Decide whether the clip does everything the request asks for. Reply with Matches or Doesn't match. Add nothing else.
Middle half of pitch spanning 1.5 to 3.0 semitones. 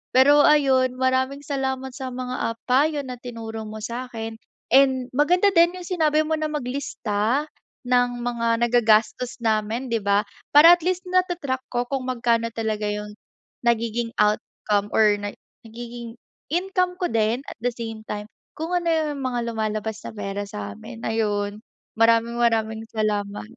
Doesn't match